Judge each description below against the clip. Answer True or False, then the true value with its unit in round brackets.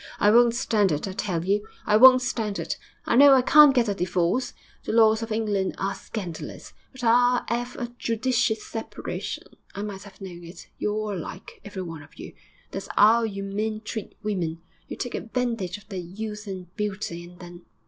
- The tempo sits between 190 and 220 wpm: True (195 wpm)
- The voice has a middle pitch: False (210 Hz)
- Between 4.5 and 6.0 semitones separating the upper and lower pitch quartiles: False (3.6 semitones)